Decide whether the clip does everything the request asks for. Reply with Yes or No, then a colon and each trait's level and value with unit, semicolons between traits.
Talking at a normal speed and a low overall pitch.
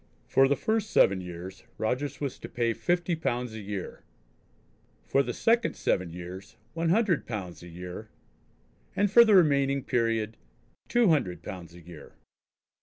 Yes: average, 155 wpm; low, 120 Hz